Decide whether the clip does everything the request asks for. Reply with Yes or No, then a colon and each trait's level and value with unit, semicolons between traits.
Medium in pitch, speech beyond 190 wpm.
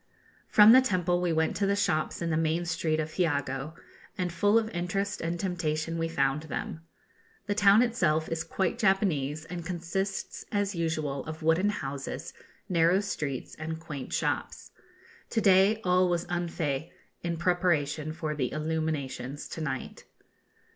No: medium, 165 Hz; average, 155 wpm